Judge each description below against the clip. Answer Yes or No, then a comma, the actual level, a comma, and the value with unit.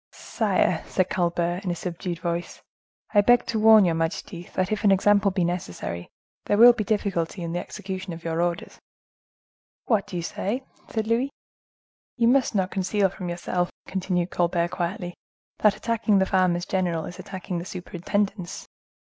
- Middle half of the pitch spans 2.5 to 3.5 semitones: Yes, average, 3.0 semitones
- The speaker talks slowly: No, average, 165 wpm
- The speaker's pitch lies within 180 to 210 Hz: Yes, medium, 185 Hz